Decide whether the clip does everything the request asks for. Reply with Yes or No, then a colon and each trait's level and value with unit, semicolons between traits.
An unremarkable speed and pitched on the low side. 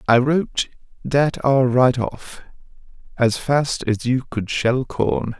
Yes: average, 145 wpm; low, 125 Hz